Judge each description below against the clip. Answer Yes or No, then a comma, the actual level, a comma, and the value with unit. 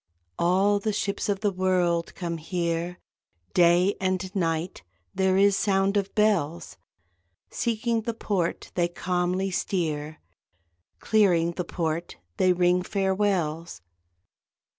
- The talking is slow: Yes, slow, 115 wpm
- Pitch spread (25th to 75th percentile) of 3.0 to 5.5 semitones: No, narrow, 2.6 semitones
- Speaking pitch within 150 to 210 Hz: Yes, medium, 185 Hz